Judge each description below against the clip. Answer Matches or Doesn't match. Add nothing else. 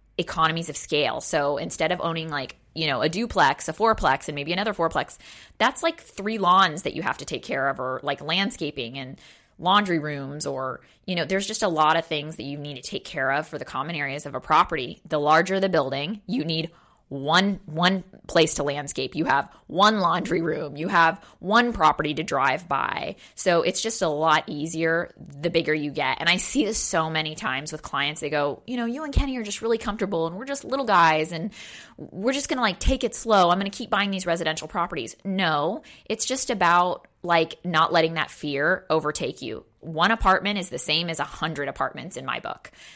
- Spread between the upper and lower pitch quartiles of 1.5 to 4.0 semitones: Doesn't match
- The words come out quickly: Matches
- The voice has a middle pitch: Matches